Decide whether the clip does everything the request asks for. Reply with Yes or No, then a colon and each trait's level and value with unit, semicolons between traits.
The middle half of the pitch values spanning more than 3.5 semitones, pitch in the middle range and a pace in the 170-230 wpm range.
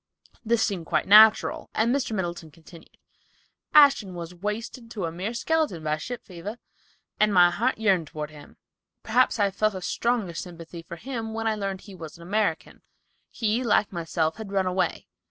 No: average, 4.6 semitones; high, 200 Hz; average, 180 wpm